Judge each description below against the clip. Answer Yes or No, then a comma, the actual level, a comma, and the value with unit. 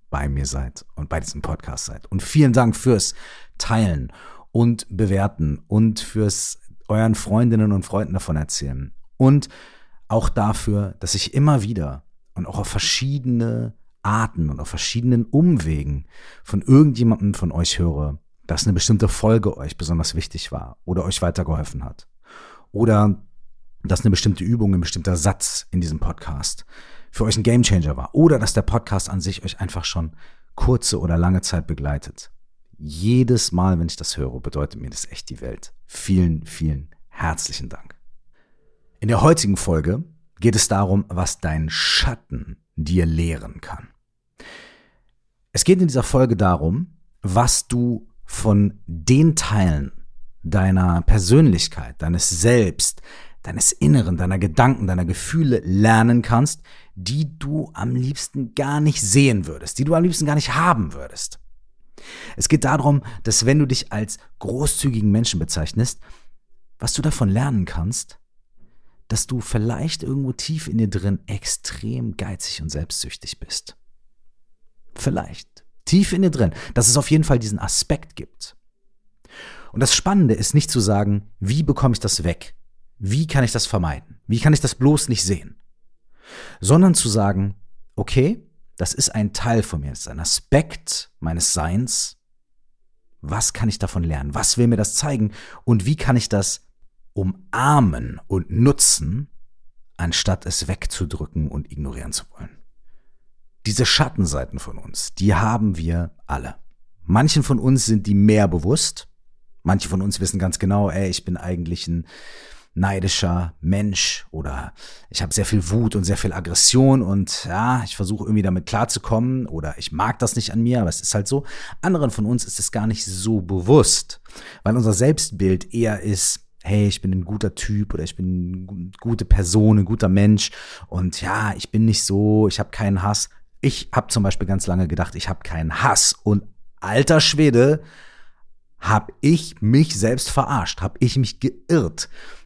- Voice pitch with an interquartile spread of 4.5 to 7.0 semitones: Yes, average, 5.2 semitones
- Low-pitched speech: Yes, low, 100 Hz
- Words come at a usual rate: Yes, average, 160 wpm